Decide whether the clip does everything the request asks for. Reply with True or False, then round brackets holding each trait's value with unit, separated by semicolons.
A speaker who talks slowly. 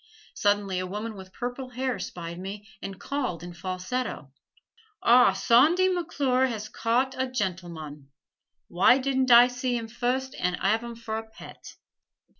False (150 wpm)